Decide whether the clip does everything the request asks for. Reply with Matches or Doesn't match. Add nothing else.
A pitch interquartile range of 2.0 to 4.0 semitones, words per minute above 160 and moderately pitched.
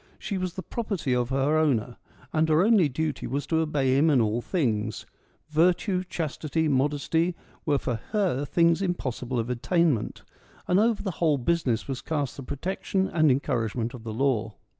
Doesn't match